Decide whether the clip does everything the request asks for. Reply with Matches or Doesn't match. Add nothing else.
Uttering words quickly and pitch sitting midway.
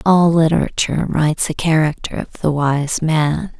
Doesn't match